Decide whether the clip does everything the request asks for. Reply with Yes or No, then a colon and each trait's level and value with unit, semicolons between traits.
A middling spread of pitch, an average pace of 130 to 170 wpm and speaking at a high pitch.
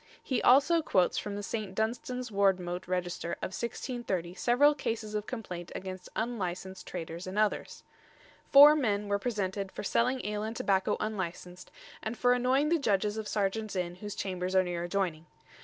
Yes: average, 4.2 semitones; average, 165 wpm; high, 205 Hz